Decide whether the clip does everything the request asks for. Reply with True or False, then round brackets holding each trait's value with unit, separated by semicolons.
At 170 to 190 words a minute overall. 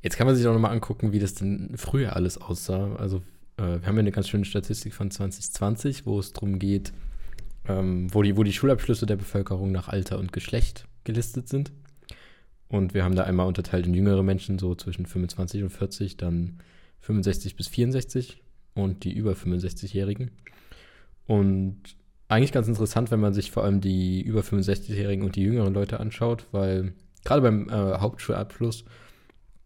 True (175 wpm)